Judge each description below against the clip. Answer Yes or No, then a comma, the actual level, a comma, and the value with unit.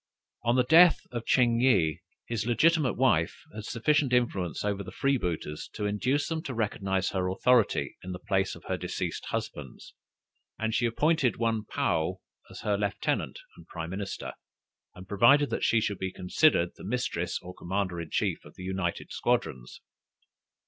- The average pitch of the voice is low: Yes, low, 105 Hz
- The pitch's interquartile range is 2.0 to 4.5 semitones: No, average, 5.3 semitones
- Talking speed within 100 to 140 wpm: No, average, 165 wpm